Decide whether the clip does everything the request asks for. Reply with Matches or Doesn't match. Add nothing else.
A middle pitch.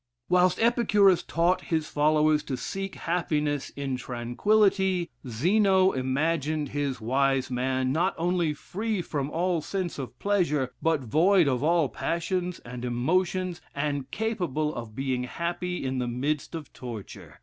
Matches